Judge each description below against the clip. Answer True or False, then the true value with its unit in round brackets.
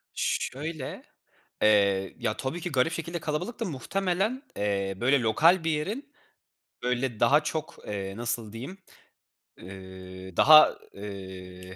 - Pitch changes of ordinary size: False (8.8 semitones)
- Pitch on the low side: True (125 Hz)